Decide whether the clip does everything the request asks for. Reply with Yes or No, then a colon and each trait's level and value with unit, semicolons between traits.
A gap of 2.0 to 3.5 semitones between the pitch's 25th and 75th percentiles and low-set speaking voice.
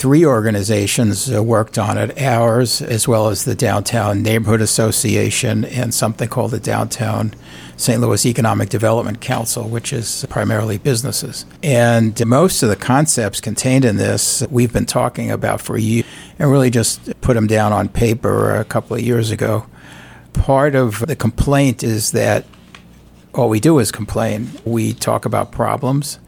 Yes: narrow, 2.5 semitones; low, 115 Hz